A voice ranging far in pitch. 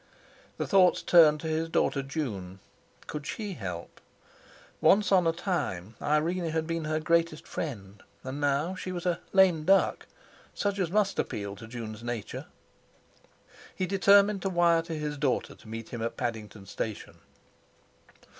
Yes: wide, 7.4 semitones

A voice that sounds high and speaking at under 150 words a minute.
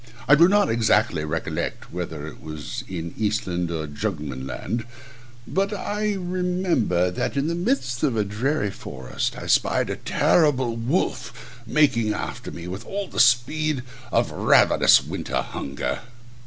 No: low, 115 Hz; average, 140 wpm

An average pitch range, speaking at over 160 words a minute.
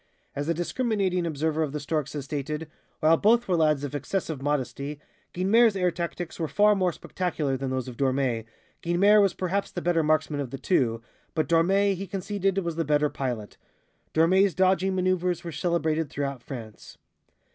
Yes: average, 4.5 semitones; average, 175 wpm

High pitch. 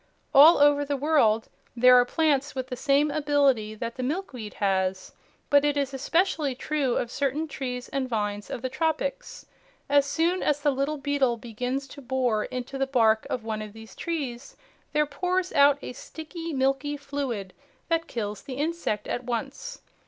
Yes: very high, 275 Hz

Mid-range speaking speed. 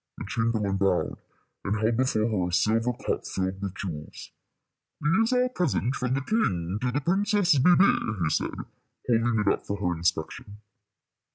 Yes: average, 170 wpm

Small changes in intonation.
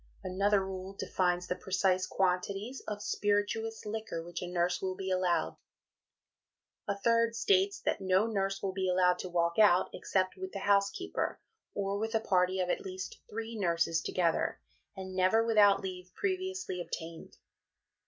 Yes: narrow, 2.2 semitones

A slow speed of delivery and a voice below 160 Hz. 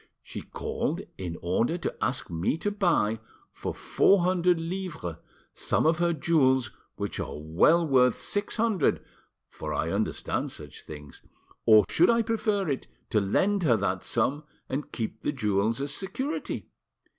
No: average, 155 wpm; medium, 140 Hz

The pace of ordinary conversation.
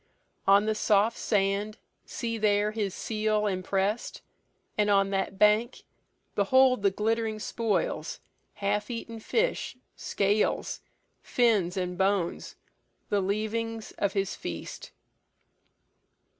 No: slow, 105 wpm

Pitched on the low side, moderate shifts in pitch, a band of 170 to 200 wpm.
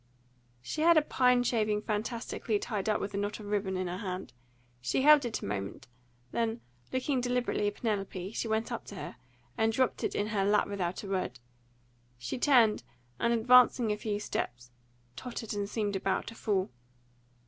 No: high, 210 Hz; average, 3.3 semitones; average, 180 wpm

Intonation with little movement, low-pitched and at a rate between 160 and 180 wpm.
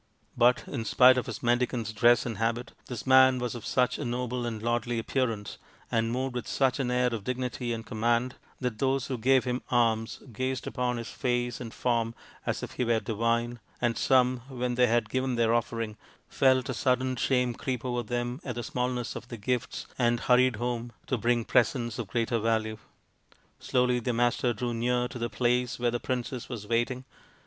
No: narrow, 1.3 semitones; low, 120 Hz; average, 195 wpm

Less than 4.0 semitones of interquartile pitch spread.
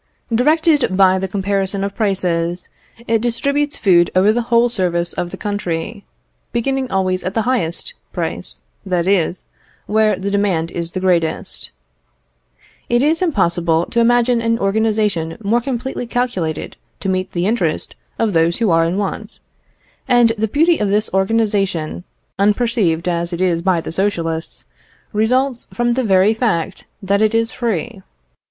No: average, 4.7 semitones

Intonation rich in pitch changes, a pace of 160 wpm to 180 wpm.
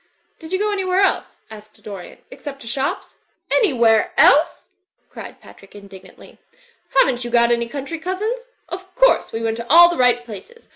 Yes: wide, 8.3 semitones; average, 165 wpm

